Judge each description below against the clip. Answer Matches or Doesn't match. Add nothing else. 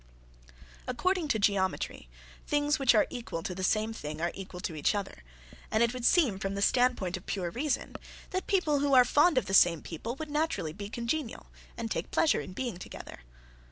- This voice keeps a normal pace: Matches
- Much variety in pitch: Matches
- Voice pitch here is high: Matches